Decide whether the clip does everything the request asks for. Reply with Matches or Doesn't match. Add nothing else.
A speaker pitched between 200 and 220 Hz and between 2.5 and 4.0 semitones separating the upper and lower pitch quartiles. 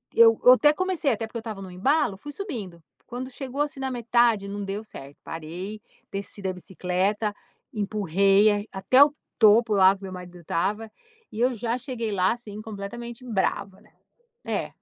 Matches